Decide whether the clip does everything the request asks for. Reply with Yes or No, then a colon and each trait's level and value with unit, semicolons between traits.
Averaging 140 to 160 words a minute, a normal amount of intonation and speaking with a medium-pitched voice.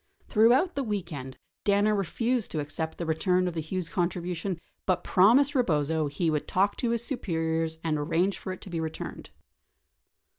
No: average, 170 wpm; average, 4.4 semitones; medium, 180 Hz